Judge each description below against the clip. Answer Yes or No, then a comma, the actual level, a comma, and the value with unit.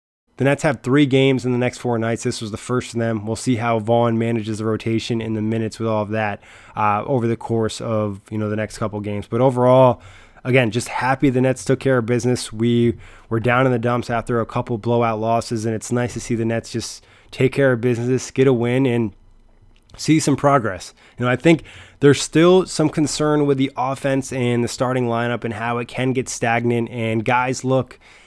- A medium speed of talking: No, fast, 225 wpm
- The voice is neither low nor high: No, low, 120 Hz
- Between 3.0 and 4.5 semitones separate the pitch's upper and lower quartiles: No, narrow, 2.5 semitones